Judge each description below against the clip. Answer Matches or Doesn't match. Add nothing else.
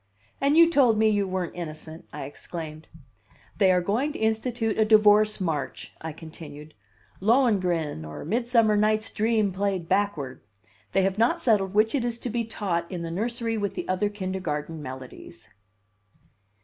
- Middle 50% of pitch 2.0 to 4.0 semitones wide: Doesn't match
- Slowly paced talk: Doesn't match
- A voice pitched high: Matches